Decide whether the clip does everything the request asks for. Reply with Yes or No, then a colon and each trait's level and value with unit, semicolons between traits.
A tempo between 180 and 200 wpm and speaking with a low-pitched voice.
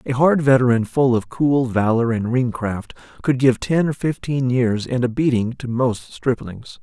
Yes: average, 195 wpm; low, 125 Hz